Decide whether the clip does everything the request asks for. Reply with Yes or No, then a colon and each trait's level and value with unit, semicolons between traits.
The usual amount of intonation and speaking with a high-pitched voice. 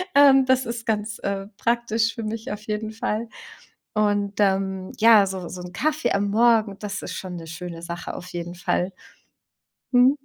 Yes: average, 3.3 semitones; high, 210 Hz